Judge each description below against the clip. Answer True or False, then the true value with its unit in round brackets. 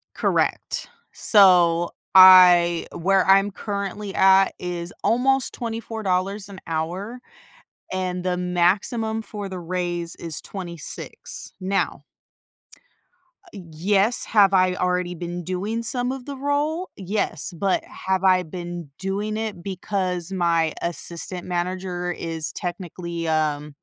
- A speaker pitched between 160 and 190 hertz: True (185 Hz)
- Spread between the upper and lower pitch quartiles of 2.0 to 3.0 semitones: True (2.6 semitones)